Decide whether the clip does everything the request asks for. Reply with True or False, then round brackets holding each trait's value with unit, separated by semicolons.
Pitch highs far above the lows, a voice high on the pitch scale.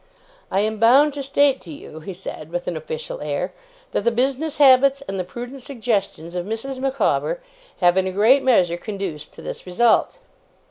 True (6.8 semitones; 230 Hz)